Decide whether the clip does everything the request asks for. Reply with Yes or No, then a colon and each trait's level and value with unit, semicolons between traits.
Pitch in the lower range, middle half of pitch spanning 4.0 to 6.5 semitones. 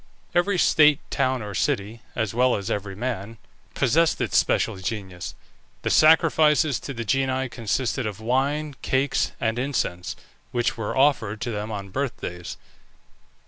Yes: low, 120 Hz; average, 4.9 semitones